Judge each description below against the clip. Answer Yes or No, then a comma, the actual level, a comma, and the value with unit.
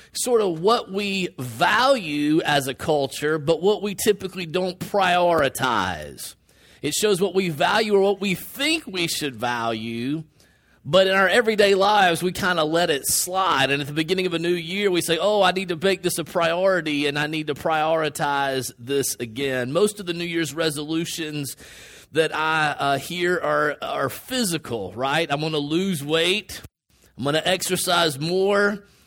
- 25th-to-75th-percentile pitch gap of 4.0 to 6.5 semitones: Yes, average, 4.3 semitones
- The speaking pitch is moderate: Yes, medium, 170 Hz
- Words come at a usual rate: Yes, average, 185 wpm